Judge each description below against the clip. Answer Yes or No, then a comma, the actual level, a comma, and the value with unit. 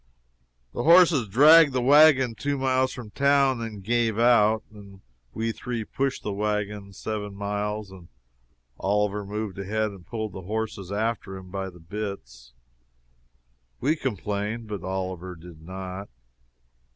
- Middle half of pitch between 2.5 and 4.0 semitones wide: Yes, average, 3.4 semitones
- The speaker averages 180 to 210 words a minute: No, average, 140 wpm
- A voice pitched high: No, low, 105 Hz